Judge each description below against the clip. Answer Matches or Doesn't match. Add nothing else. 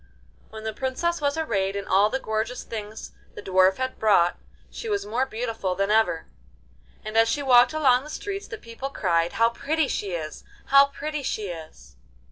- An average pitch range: Doesn't match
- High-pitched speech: Matches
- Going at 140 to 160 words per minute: Doesn't match